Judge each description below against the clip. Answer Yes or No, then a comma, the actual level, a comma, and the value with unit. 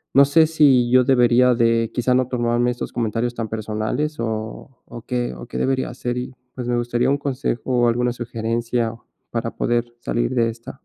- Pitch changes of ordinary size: No, narrow, 1.6 semitones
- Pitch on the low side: Yes, low, 120 Hz